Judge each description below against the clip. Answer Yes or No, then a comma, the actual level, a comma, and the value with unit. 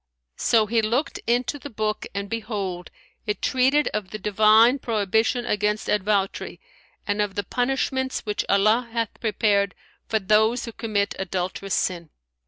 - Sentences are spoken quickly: No, average, 145 wpm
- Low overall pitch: No, high, 215 Hz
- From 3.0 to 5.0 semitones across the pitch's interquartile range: No, narrow, 2.6 semitones